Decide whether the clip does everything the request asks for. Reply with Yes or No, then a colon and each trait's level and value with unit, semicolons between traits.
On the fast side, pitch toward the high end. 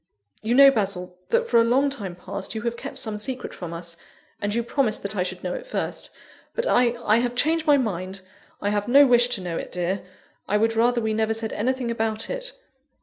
Yes: fast, 225 wpm; high, 225 Hz